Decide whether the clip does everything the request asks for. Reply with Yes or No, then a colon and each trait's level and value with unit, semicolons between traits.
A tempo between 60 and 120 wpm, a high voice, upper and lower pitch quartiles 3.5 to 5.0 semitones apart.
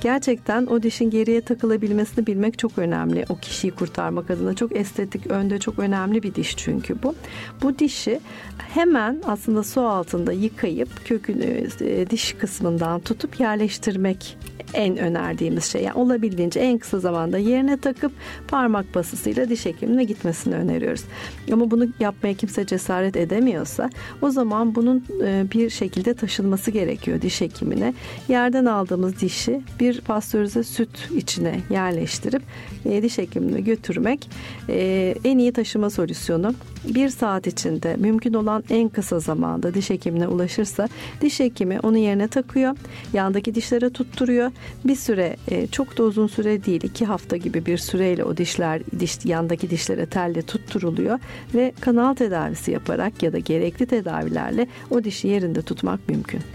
No: fast, 140 wpm; high, 220 Hz; average, 4.3 semitones